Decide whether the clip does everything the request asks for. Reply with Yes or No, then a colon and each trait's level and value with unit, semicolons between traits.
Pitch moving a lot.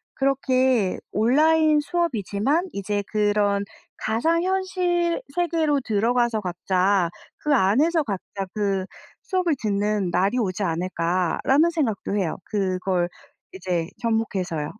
Yes: wide, 7.8 semitones